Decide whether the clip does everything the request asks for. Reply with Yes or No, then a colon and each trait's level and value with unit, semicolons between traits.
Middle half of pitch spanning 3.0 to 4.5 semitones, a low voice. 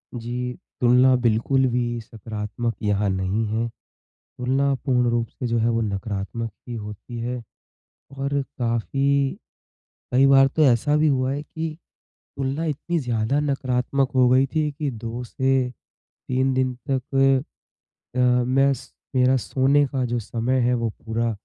No: narrow, 2.6 semitones; low, 125 Hz